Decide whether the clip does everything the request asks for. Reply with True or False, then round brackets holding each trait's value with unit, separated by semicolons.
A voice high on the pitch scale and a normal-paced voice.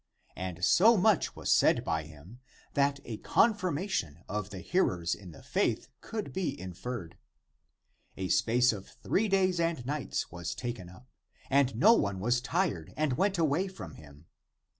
False (125 Hz; 160 wpm)